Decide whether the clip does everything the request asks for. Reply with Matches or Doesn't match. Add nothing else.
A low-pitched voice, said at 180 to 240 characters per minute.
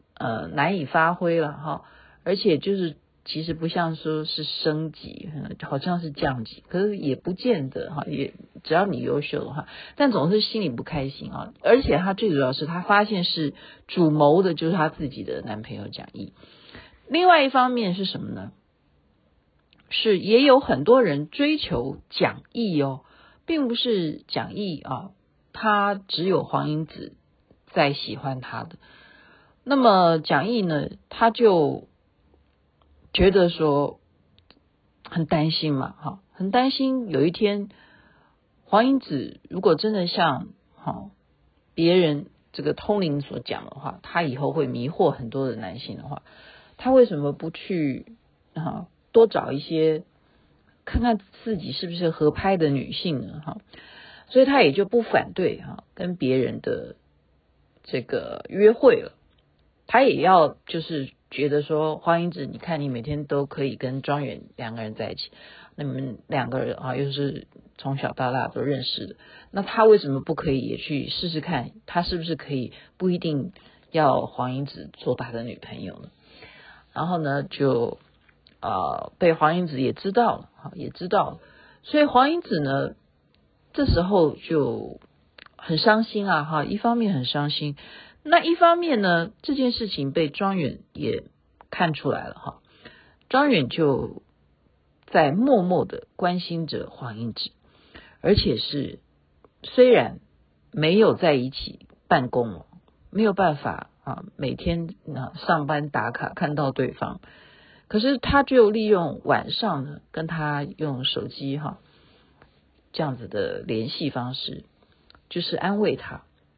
Doesn't match